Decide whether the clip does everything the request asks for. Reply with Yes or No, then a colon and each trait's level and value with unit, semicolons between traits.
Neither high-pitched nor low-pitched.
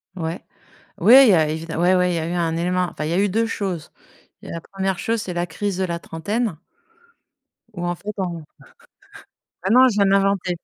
Yes: medium, 180 Hz